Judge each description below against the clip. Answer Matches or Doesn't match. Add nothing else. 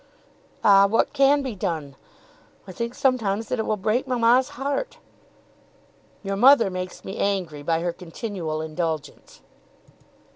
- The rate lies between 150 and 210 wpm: Doesn't match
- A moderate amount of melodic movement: Doesn't match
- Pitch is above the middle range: Matches